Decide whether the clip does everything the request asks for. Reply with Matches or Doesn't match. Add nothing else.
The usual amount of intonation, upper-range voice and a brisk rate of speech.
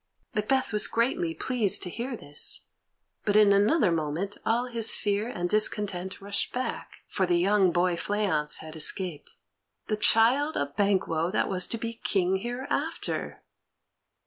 Doesn't match